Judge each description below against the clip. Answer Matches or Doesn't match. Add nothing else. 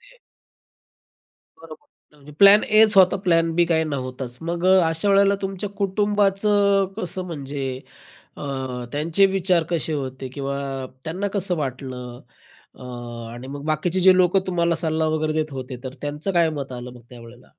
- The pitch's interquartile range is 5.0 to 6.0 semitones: Matches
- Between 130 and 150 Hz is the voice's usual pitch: Doesn't match